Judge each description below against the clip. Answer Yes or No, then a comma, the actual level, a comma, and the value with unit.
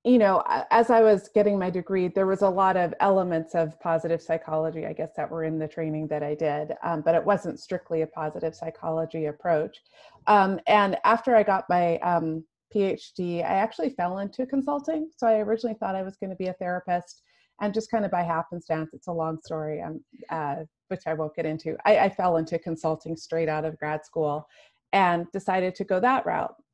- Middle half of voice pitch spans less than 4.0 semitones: Yes, average, 3.6 semitones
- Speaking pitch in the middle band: Yes, medium, 175 Hz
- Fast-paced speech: Yes, fast, 210 wpm